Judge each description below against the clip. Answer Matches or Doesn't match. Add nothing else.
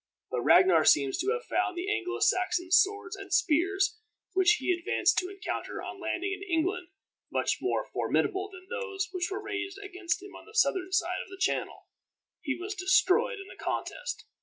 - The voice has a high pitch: Matches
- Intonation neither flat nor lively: Doesn't match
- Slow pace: Doesn't match